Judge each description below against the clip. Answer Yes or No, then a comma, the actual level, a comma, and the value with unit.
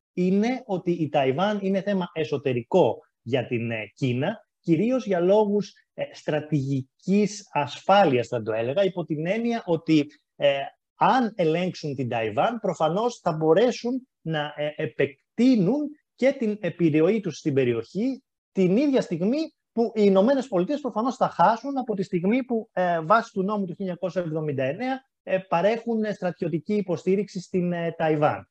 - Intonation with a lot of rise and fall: Yes, wide, 5.8 semitones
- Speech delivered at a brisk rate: No, average, 135 wpm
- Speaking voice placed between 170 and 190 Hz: Yes, medium, 185 Hz